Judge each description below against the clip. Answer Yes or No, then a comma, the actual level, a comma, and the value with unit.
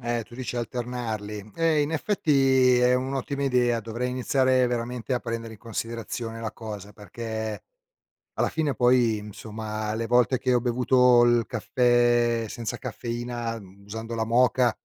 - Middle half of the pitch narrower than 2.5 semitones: Yes, narrow, 1.9 semitones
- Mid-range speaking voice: No, low, 120 Hz